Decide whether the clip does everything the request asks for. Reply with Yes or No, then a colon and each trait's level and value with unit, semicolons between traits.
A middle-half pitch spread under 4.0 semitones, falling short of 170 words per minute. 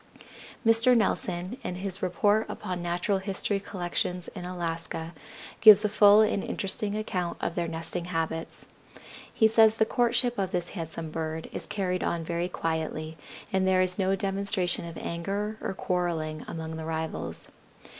Yes: average, 3.4 semitones; average, 155 wpm